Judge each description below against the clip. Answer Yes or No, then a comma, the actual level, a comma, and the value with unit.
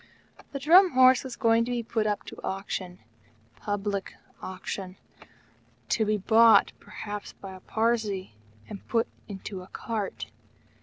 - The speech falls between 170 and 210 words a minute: No, average, 140 wpm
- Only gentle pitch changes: No, average, 3.0 semitones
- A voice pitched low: No, high, 215 Hz